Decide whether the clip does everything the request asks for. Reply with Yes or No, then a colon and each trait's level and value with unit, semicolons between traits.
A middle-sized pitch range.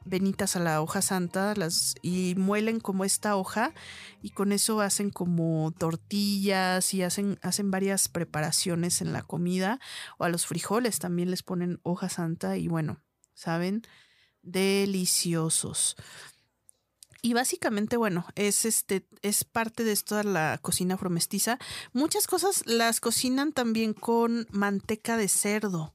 Yes: average, 3.4 semitones